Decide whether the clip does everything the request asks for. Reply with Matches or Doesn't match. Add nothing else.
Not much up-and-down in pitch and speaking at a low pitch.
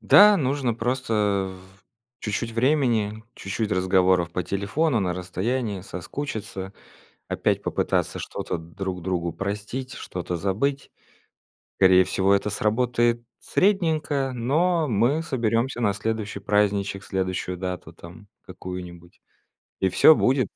Doesn't match